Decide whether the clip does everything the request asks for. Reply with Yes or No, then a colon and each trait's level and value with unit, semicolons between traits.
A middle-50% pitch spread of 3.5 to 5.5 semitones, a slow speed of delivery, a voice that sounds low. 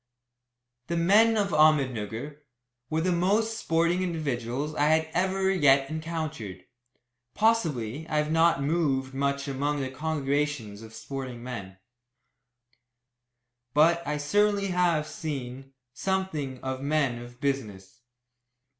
No: average, 4.3 semitones; slow, 120 wpm; medium, 150 Hz